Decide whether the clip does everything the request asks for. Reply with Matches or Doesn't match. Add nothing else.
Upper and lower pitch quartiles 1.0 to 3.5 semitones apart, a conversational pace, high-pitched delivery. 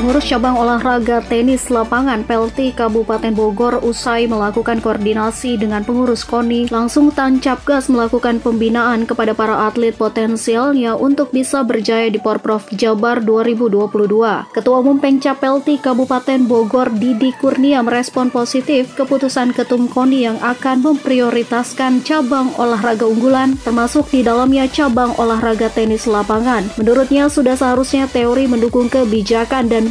Matches